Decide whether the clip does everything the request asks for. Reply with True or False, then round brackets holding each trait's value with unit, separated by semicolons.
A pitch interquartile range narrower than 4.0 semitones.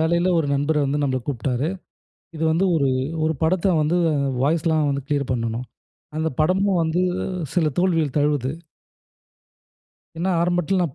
True (3.4 semitones)